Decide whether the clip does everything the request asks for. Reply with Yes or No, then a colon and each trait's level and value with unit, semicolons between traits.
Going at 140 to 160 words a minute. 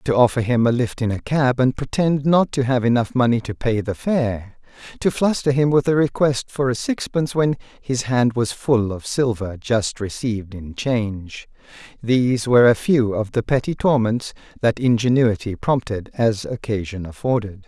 No: average, 180 wpm